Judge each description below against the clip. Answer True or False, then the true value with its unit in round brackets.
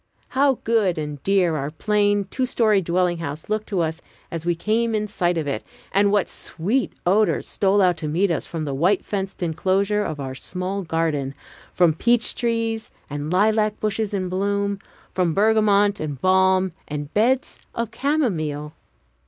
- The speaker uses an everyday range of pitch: True (4.6 semitones)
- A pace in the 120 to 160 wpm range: False (170 wpm)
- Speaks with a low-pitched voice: False (190 Hz)